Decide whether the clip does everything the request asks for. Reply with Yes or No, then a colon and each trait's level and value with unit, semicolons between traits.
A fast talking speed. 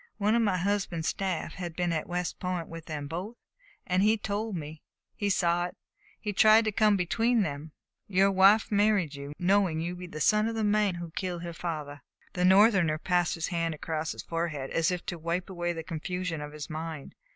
Yes: fast, 210 wpm